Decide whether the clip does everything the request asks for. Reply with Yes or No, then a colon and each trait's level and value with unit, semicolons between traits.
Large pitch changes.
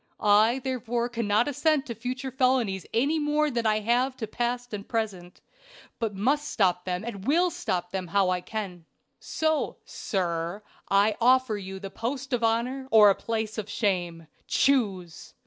No: average, 4.7 semitones